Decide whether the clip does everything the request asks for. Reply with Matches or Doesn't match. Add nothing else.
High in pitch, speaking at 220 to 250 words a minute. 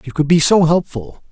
Doesn't match